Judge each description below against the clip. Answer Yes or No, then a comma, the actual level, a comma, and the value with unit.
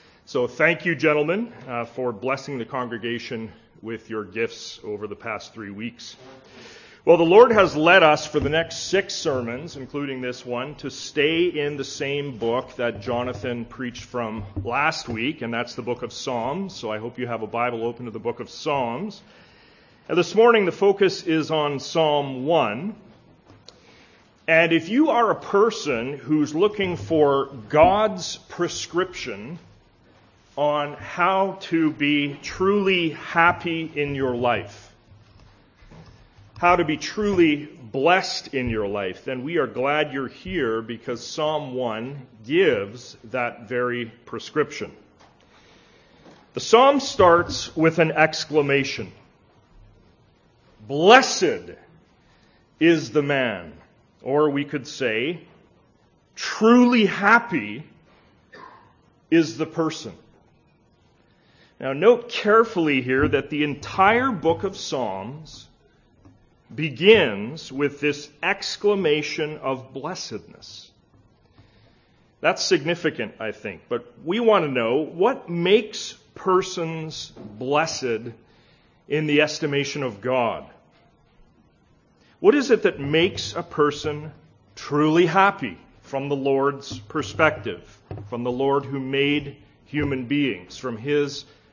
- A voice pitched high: No, medium, 145 Hz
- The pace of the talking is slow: Yes, slow, 120 wpm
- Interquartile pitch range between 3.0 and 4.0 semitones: No, wide, 5.4 semitones